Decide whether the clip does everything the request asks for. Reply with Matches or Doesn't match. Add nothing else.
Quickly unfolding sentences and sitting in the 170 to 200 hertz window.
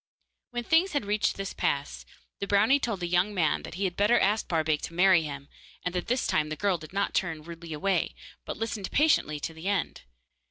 Matches